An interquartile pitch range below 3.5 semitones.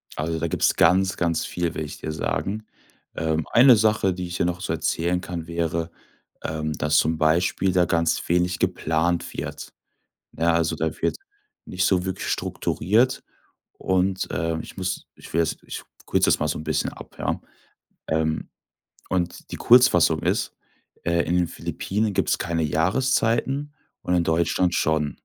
Yes: narrow, 2.5 semitones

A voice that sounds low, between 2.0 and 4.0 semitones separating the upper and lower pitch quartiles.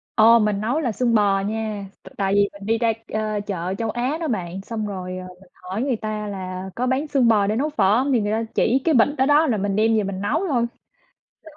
No: high, 215 Hz; average, 3.4 semitones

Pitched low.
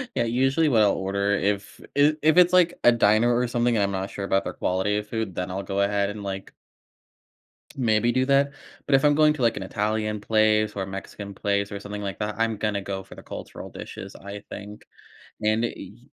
Yes: low, 105 Hz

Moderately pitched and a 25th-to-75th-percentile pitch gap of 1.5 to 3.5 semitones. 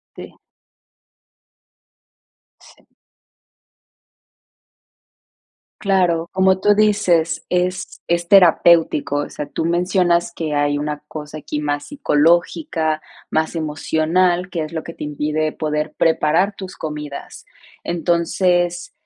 Yes: medium, 165 Hz; average, 2.8 semitones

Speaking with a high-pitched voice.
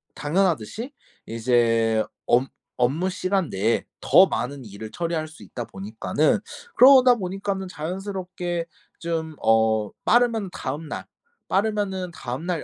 No: medium, 165 Hz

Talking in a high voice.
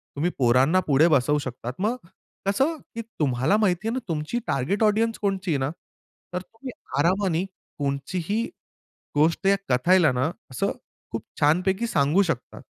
No: medium, 170 Hz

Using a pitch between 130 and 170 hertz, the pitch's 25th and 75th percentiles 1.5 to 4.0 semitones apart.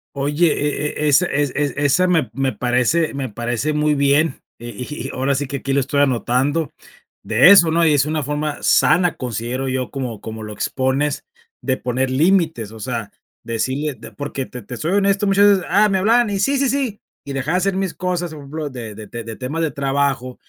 No: medium, 140 Hz; average, 4.5 semitones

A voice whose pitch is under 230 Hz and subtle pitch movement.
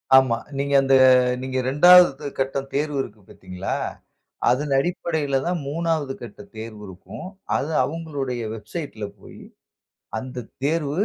No: low, 135 Hz; average, 4.0 semitones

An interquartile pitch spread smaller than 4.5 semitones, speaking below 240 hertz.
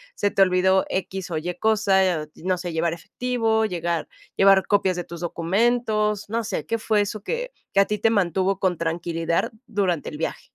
Yes: average, 3.6 semitones; high, 190 Hz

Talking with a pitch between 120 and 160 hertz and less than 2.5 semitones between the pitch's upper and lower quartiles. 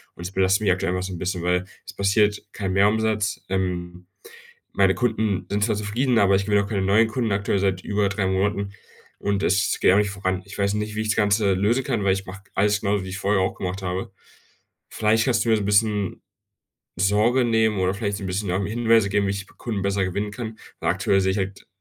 No: low, 100 Hz; narrow, 1.8 semitones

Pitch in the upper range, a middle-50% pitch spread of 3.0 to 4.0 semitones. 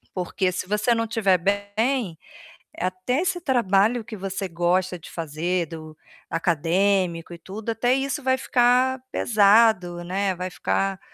No: high, 195 Hz; average, 4.5 semitones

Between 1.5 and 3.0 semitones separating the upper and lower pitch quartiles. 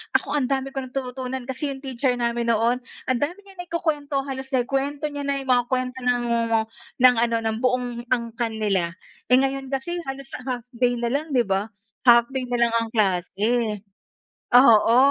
Yes: narrow, 2.5 semitones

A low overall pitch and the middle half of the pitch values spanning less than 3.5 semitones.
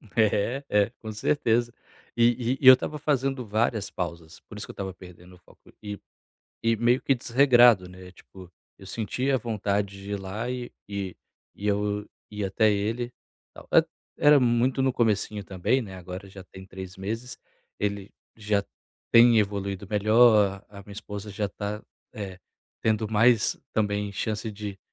Yes: low, 105 Hz; average, 3.1 semitones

